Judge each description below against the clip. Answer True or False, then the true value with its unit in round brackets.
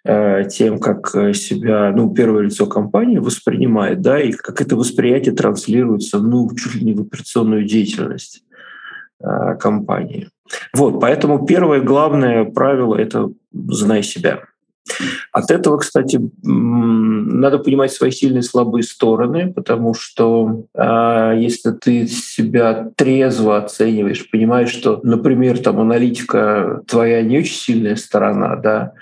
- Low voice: True (115 Hz)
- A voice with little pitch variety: True (2.0 semitones)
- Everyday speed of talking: True (120 wpm)